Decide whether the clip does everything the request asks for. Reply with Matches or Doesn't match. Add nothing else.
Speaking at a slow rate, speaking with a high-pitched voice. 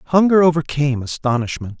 Doesn't match